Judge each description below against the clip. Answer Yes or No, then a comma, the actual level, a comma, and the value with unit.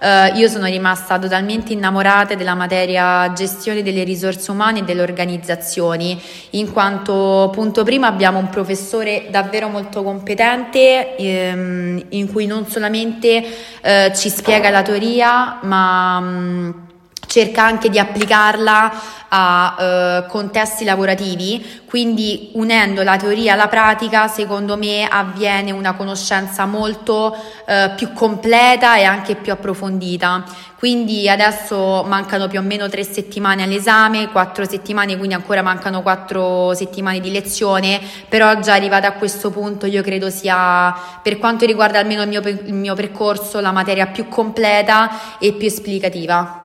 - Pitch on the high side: Yes, high, 200 Hz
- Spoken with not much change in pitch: Yes, narrow, 2.3 semitones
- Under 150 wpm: Yes, average, 140 wpm